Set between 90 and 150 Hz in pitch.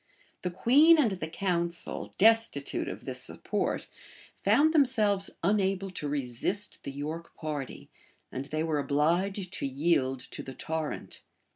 No: medium, 170 Hz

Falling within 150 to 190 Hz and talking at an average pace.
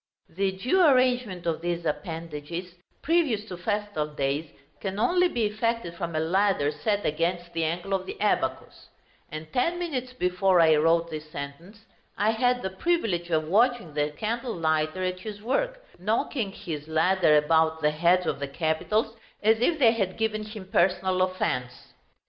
Yes: medium, 185 Hz; average, 160 wpm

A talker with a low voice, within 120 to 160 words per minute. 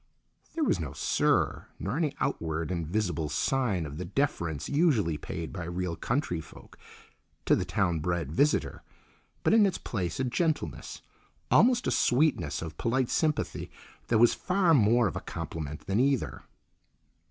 Yes: low, 100 Hz; average, 155 wpm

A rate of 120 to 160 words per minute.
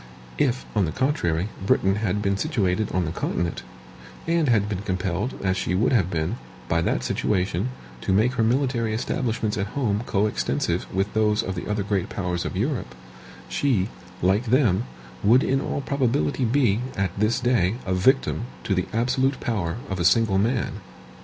No: average, 170 wpm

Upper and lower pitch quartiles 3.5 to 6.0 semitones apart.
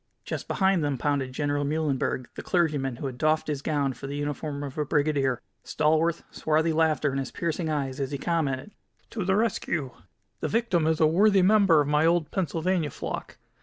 No: average, 3.0 semitones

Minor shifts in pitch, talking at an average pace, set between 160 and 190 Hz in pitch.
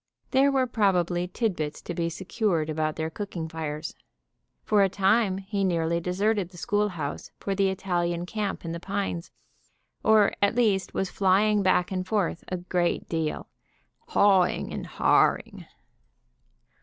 No: average, 3.1 semitones; average, 145 wpm; medium, 185 Hz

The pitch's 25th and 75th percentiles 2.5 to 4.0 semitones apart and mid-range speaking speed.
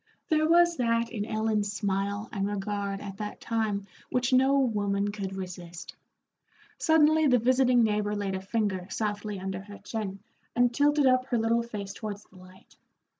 Yes: average, 3.6 semitones; average, 165 wpm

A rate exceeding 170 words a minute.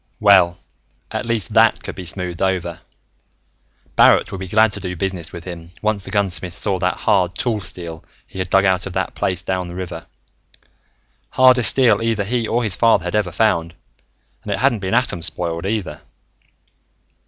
Yes: average, 180 wpm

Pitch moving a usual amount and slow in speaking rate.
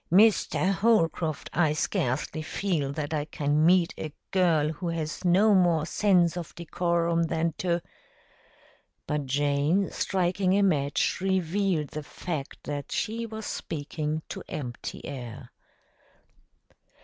Yes: average, 3.7 semitones; slow, 125 wpm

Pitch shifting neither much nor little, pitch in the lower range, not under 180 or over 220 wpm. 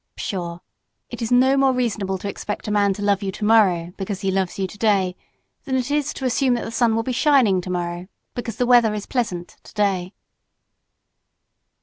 No: average, 4.4 semitones; high, 210 Hz; average, 190 wpm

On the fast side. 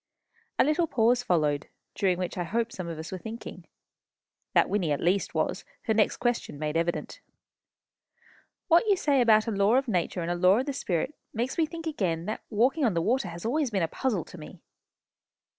Yes: fast, 210 wpm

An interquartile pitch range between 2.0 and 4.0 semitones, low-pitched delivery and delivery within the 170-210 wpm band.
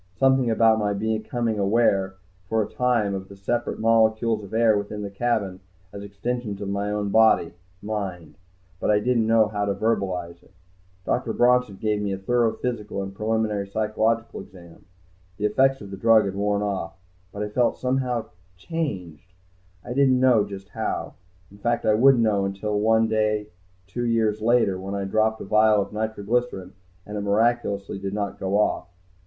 Yes: narrow, 2.4 semitones; low, 105 Hz; average, 180 wpm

